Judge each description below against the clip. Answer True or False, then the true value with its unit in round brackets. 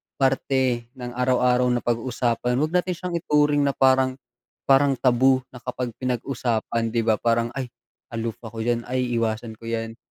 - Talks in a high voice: False (125 Hz)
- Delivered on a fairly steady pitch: True (2.2 semitones)